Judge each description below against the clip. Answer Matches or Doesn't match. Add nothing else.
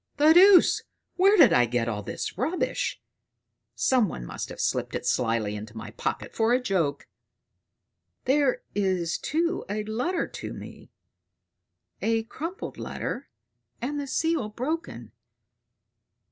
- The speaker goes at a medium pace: Doesn't match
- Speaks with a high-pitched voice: Matches